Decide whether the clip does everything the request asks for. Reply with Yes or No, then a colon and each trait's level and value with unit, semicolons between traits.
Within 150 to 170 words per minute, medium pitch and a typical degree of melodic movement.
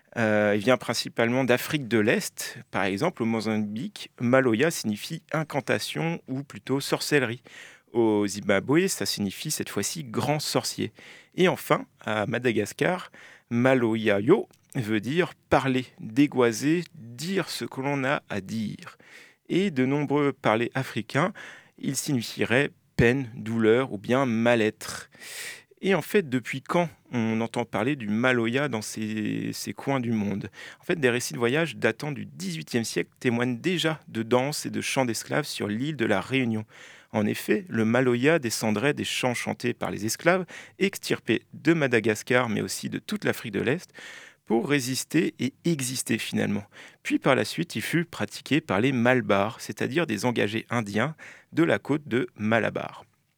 No: average, 155 wpm; low, 125 Hz; average, 4.6 semitones